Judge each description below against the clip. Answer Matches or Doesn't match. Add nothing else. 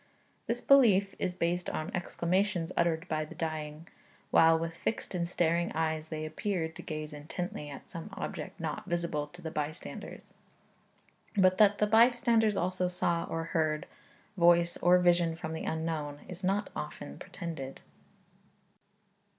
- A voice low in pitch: Doesn't match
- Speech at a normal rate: Matches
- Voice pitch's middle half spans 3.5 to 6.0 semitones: Doesn't match